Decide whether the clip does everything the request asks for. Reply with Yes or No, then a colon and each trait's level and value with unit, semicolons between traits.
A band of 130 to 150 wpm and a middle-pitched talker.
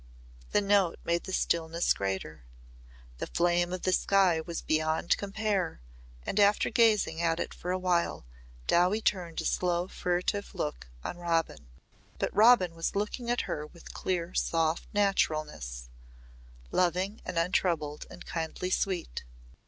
Yes: average, 140 wpm; medium, 175 Hz